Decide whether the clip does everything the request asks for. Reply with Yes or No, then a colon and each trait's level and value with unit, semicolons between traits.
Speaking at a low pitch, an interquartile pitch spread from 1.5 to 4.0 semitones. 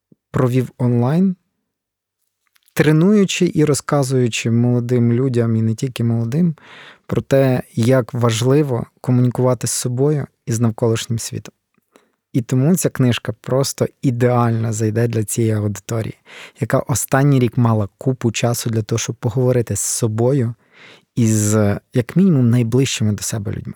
Yes: low, 125 Hz; average, 2.8 semitones